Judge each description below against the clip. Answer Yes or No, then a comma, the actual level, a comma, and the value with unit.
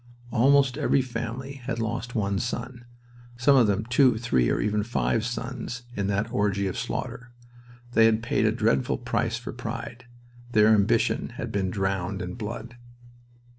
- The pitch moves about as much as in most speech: Yes, average, 3.4 semitones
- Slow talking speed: No, average, 155 wpm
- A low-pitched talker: Yes, low, 115 Hz